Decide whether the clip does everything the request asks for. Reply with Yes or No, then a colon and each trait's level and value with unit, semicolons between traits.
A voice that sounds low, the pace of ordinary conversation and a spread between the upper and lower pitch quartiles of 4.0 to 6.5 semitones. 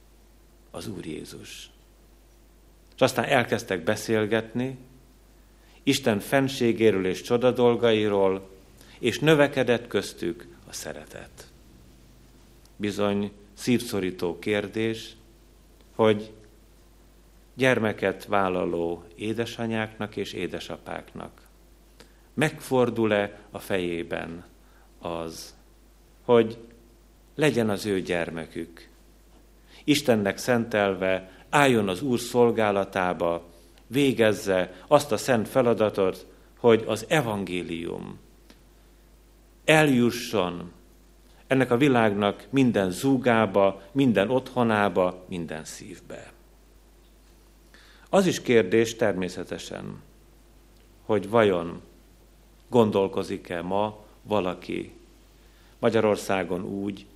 No: low, 105 Hz; slow, 70 wpm; average, 4.4 semitones